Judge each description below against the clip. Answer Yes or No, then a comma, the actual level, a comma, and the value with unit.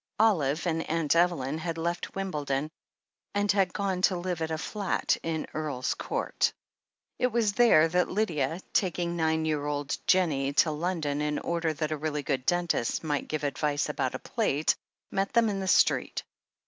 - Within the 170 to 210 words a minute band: Yes, average, 175 wpm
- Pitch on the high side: No, medium, 160 Hz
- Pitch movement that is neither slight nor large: Yes, average, 3.7 semitones